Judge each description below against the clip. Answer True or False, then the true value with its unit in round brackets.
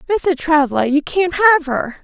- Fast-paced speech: False (175 wpm)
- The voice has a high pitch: True (310 Hz)